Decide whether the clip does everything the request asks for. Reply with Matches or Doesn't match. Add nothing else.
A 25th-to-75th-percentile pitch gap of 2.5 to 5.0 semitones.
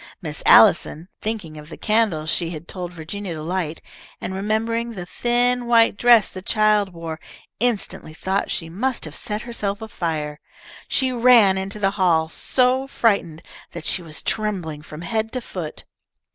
Doesn't match